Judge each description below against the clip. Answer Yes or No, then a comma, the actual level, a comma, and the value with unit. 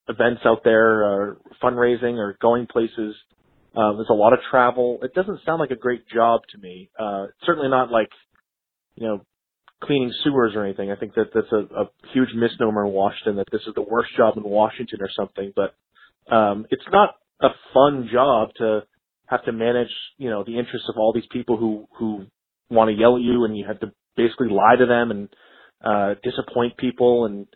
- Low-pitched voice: Yes, low, 115 Hz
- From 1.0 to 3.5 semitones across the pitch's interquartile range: Yes, narrow, 2.5 semitones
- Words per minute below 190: No, average, 200 wpm